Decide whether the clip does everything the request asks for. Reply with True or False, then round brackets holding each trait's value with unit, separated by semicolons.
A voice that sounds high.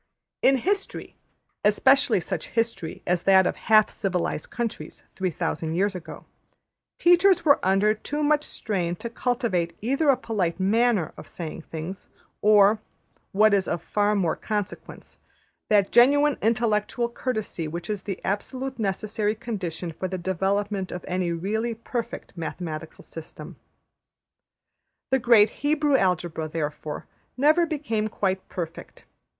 True (205 Hz)